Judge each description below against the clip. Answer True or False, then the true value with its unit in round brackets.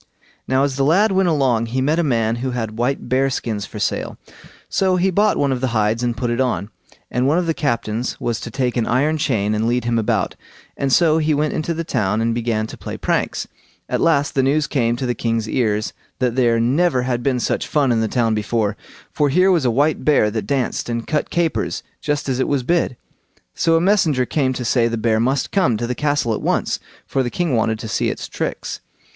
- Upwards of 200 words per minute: True (235 wpm)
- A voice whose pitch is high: False (125 Hz)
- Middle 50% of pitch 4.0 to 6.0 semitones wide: True (4.3 semitones)